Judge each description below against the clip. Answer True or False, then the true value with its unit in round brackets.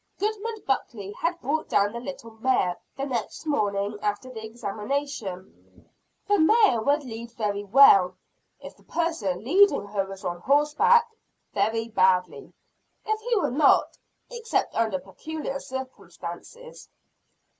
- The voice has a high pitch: True (240 Hz)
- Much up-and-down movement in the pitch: True (7.5 semitones)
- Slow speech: True (130 wpm)